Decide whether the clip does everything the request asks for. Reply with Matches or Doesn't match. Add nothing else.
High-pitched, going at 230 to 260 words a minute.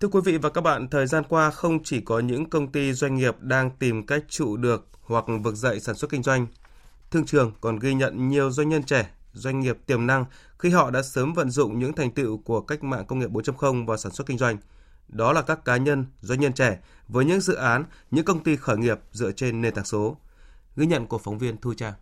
Doesn't match